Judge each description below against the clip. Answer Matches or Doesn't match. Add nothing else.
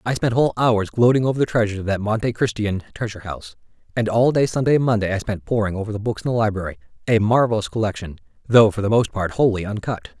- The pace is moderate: Doesn't match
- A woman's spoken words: Doesn't match